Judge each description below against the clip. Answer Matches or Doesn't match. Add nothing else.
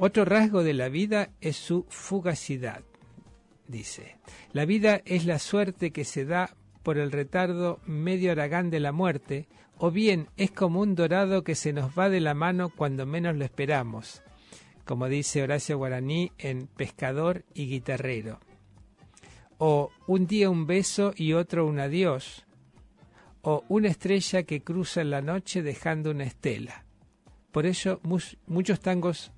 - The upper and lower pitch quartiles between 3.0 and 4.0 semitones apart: Doesn't match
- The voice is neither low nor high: Matches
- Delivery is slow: Doesn't match